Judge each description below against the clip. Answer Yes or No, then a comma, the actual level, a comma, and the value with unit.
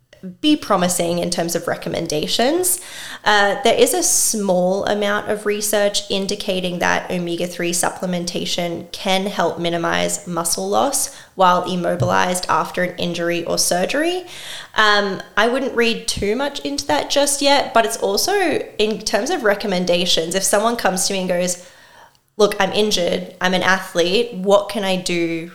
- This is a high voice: Yes, high, 195 Hz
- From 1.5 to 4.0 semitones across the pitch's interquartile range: Yes, average, 3.3 semitones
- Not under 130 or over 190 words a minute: Yes, average, 155 wpm